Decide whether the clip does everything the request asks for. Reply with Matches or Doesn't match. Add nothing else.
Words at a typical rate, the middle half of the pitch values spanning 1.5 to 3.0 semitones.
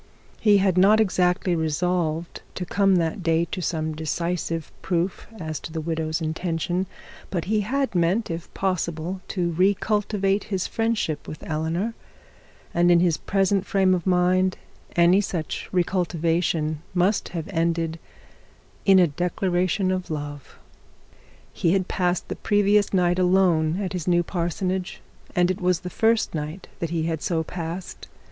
Matches